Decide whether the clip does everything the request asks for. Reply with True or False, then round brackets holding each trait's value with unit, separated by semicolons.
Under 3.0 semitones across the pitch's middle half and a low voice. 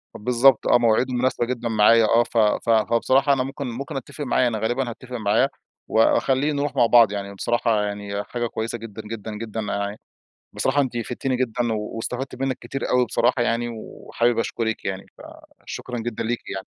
True (2.4 semitones; 120 Hz)